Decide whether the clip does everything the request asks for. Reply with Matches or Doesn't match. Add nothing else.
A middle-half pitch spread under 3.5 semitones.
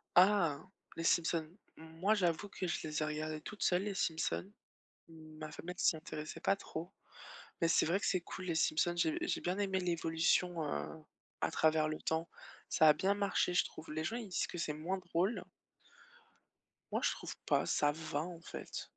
Matches